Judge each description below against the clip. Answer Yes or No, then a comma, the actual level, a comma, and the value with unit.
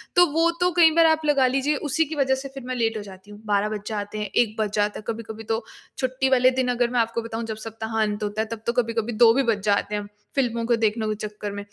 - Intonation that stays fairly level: No, average, 3.5 semitones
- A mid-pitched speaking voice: No, high, 230 Hz